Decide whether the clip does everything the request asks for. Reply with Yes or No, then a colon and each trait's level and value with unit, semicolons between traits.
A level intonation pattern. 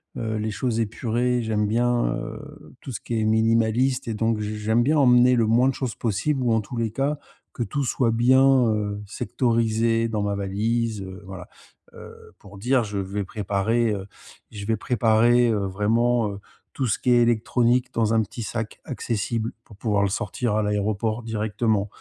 Yes: narrow, 2.3 semitones